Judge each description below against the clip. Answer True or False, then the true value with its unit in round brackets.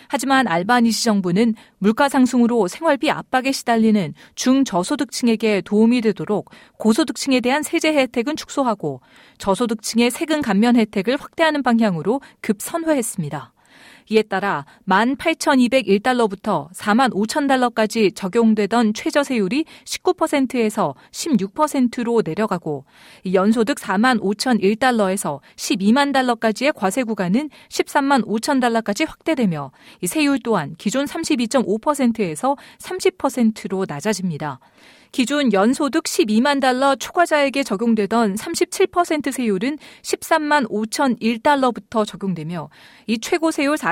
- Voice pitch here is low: False (240 Hz)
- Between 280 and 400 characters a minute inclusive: False (255 characters per minute)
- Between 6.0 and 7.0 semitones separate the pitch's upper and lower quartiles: False (5.6 semitones)